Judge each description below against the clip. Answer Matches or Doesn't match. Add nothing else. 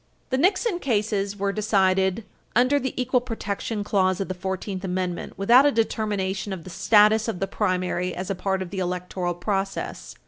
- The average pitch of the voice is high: Matches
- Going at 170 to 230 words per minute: Matches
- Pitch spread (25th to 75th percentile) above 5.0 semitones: Doesn't match